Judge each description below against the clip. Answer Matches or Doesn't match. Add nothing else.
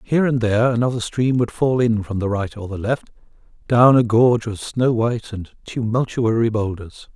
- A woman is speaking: Doesn't match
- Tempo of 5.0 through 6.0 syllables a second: Matches